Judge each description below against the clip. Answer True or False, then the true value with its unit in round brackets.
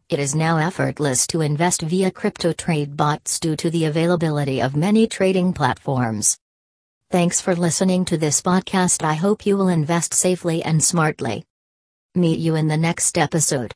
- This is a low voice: False (165 Hz)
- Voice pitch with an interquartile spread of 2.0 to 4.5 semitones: True (3.4 semitones)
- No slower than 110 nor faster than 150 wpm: False (165 wpm)